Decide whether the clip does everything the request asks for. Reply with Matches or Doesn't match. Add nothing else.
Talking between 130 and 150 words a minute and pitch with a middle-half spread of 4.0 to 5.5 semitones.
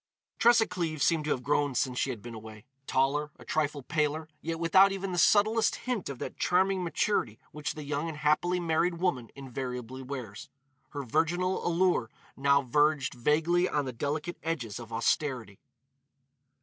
Doesn't match